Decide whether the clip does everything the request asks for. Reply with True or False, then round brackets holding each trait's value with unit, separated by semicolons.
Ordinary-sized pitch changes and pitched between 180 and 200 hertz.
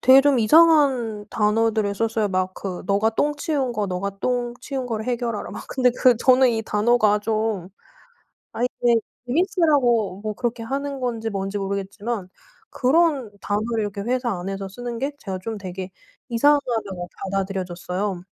False (4.0 semitones; 225 Hz)